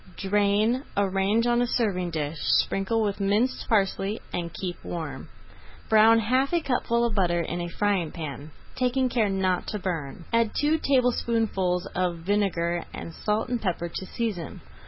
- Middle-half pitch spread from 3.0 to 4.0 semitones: No, average, 4.8 semitones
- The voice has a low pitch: No, high, 200 Hz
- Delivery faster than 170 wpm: No, average, 155 wpm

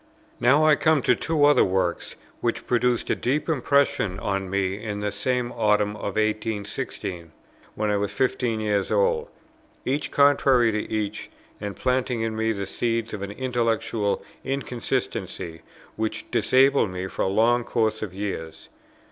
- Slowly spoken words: No, average, 155 wpm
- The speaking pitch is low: Yes, low, 110 Hz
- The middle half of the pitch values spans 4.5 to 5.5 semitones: No, average, 3.7 semitones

